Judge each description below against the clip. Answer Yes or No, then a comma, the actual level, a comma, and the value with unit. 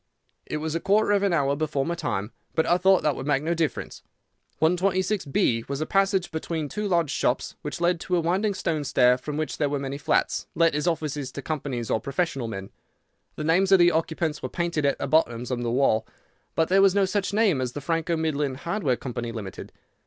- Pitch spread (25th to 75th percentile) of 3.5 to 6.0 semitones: Yes, average, 4.2 semitones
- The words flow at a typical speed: No, fast, 220 wpm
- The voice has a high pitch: No, medium, 155 Hz